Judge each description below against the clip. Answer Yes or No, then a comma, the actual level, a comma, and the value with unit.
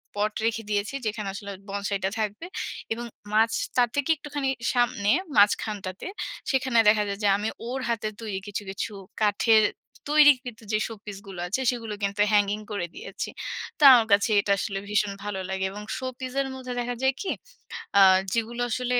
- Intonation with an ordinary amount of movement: Yes, average, 3.2 semitones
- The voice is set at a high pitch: Yes, high, 215 Hz